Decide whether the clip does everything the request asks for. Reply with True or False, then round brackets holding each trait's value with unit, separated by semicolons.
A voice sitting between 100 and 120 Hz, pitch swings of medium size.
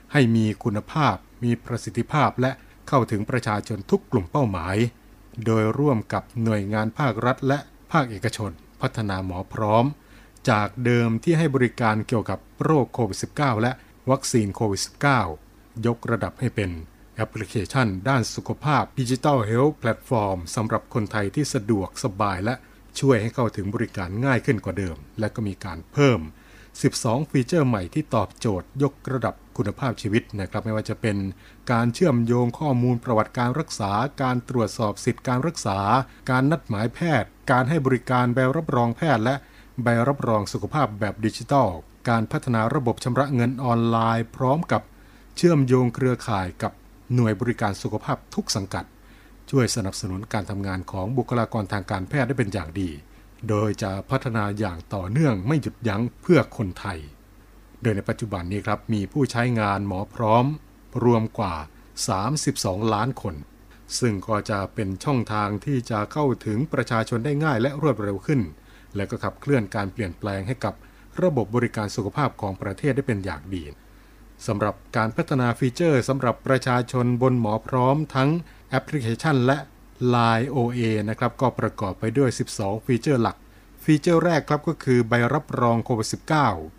True (115 Hz; 3.9 semitones)